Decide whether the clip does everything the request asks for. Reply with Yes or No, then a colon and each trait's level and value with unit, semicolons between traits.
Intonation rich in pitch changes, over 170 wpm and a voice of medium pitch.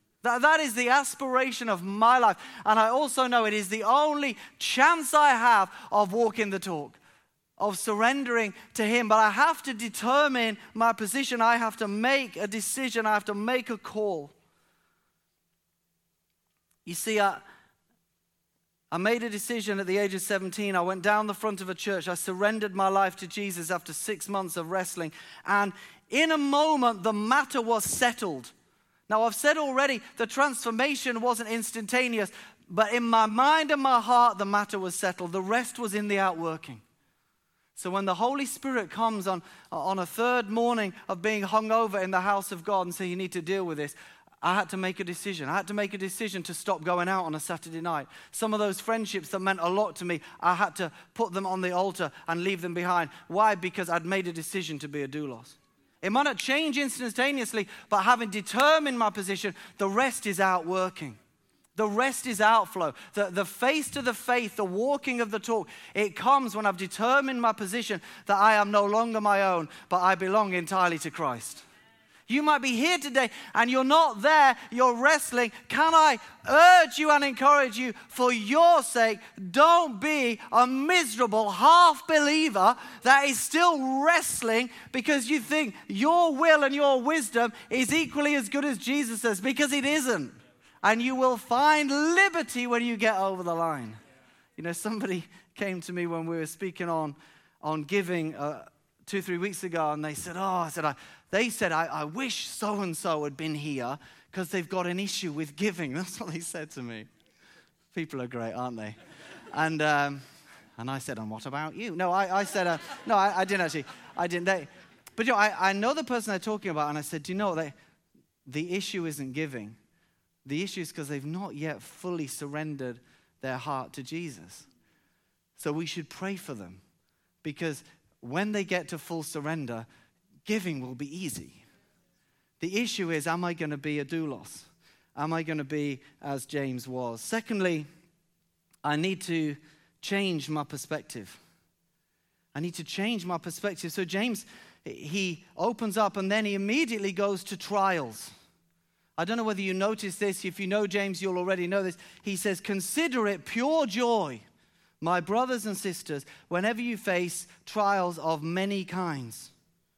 No: wide, 5.7 semitones; average, 190 wpm; high, 200 Hz